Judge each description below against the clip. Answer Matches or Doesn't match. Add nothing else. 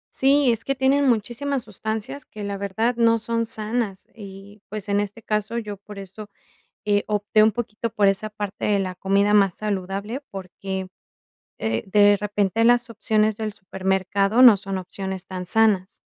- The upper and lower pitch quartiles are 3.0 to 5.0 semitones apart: Doesn't match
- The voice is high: Matches